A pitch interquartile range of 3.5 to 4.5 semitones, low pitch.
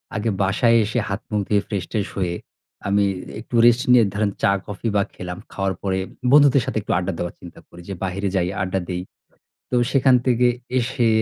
Yes: average, 3.9 semitones; low, 100 Hz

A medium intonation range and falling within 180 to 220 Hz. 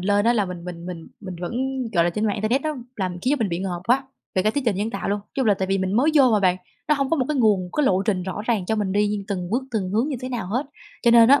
Yes: average, 4.7 semitones; high, 210 Hz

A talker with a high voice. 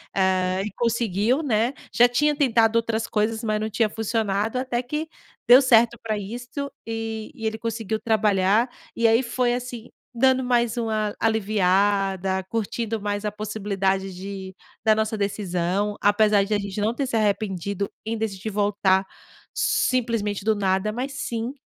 Yes: high, 220 Hz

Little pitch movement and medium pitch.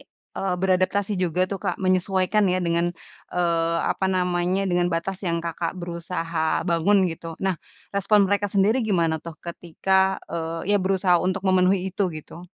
Yes: narrow, 2.2 semitones; medium, 180 Hz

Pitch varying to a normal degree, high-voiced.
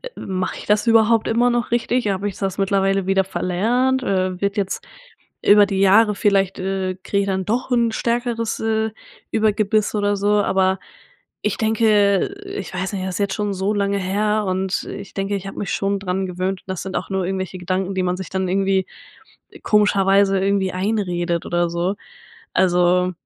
No: narrow, 1.9 semitones; high, 195 Hz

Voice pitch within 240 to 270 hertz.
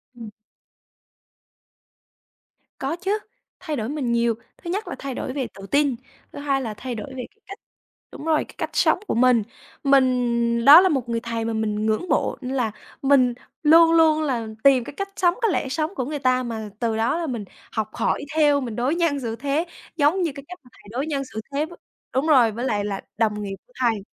Yes: very high, 260 Hz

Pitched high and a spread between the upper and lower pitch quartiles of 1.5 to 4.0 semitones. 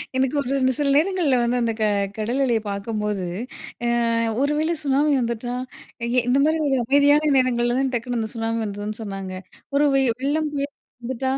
Yes: very high, 255 Hz; average, 3.7 semitones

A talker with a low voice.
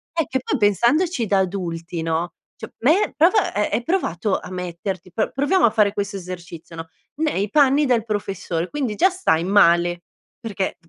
No: high, 205 Hz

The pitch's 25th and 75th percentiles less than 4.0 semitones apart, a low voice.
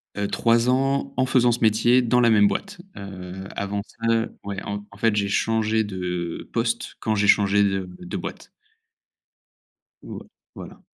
Yes: average, 2.8 semitones; low, 110 Hz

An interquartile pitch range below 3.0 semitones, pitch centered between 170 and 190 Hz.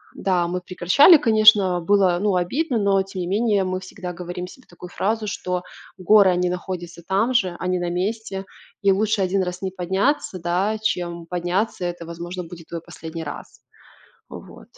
Yes: narrow, 2.4 semitones; medium, 185 Hz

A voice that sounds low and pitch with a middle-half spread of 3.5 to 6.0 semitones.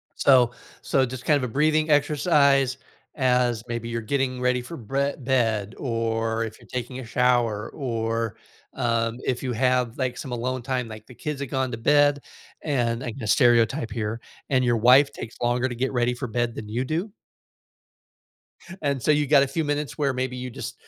No: low, 125 Hz; average, 2.8 semitones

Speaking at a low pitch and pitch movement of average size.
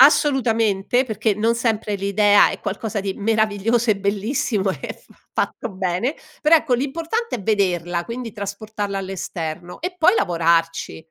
No: high, 210 Hz; average, 3.6 semitones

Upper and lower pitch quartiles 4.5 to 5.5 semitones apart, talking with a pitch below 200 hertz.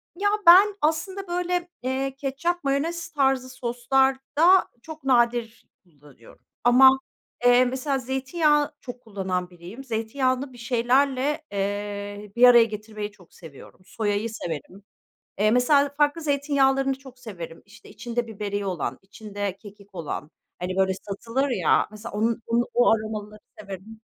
No: average, 5.0 semitones; high, 240 Hz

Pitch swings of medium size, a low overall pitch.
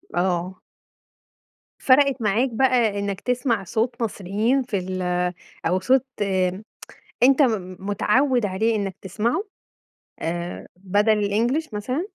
No: average, 4.7 semitones; high, 215 Hz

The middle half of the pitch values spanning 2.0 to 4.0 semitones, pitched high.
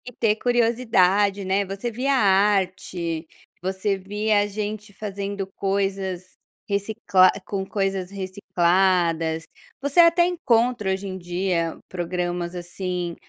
Yes: narrow, 2.4 semitones; high, 195 Hz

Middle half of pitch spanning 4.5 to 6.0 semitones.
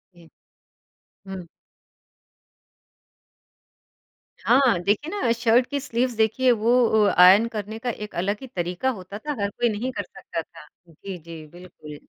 Yes: average, 5.1 semitones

